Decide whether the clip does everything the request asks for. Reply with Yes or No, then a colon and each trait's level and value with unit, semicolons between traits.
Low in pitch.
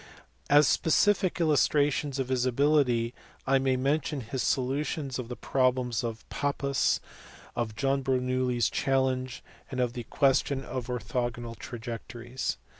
Yes: low, 130 Hz